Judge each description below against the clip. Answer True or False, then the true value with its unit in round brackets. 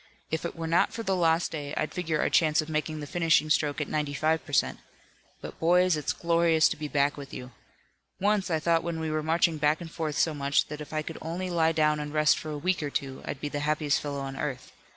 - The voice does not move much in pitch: True (2.0 semitones)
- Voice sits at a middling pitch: True (155 Hz)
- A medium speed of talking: False (255 wpm)